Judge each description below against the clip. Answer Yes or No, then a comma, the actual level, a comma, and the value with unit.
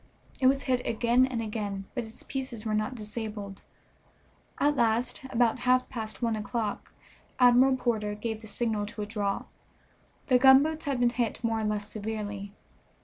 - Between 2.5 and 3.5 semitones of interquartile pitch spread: Yes, average, 3.0 semitones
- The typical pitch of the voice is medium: No, high, 230 Hz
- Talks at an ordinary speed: Yes, average, 160 wpm